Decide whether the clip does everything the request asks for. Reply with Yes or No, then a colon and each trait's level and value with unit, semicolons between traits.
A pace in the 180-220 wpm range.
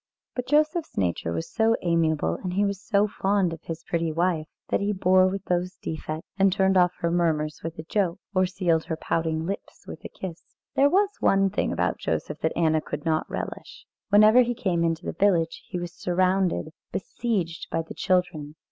Yes: average, 195 wpm